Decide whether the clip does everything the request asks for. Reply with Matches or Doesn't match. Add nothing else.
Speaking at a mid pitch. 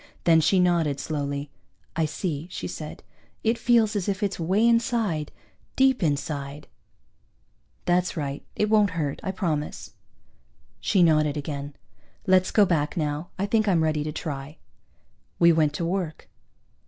Matches